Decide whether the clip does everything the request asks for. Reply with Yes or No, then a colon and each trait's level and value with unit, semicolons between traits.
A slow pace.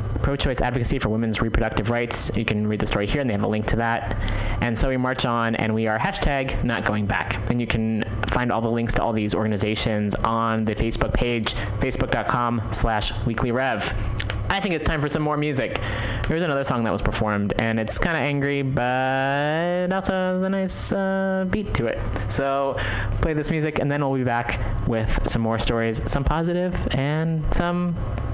No: average, 200 wpm